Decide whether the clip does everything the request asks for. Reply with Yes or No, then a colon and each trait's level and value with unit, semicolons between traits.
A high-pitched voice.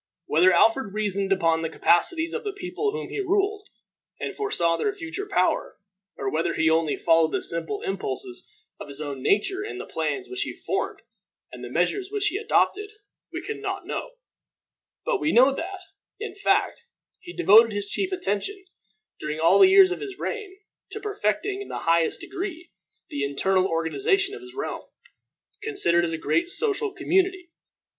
Yes: very high, 360 Hz